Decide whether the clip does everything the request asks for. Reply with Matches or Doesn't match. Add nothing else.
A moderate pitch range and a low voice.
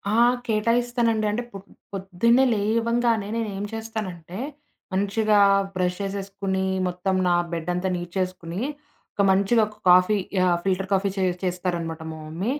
Doesn't match